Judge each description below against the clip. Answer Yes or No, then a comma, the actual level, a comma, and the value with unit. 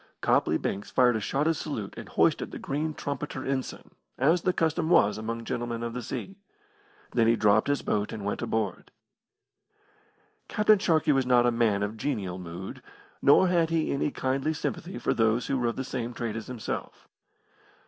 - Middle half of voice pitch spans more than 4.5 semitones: Yes, average, 5.2 semitones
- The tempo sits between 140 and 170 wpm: No, average, 185 wpm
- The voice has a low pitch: Yes, low, 125 Hz